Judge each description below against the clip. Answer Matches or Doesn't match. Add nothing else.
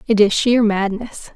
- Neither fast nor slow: Matches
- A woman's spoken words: Matches